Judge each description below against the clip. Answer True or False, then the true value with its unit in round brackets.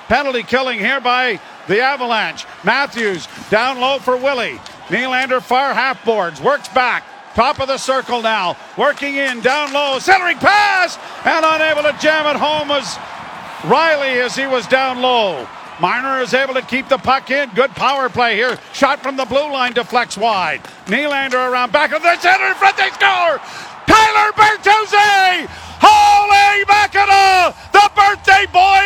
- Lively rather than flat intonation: True (6.5 semitones)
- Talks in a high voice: True (275 Hz)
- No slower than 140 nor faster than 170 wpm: True (160 wpm)